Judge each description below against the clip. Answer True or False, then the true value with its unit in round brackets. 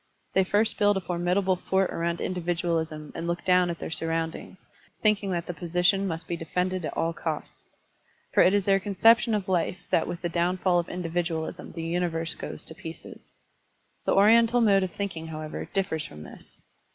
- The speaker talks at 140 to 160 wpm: False (180 wpm)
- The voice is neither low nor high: True (175 Hz)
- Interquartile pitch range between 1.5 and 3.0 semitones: True (2.7 semitones)